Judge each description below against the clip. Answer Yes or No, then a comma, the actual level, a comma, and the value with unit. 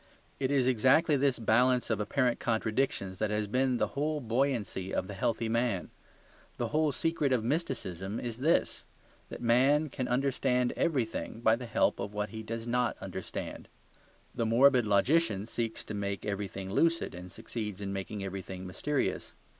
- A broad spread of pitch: No, average, 4.4 semitones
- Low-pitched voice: Yes, low, 115 Hz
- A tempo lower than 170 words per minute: Yes, average, 160 wpm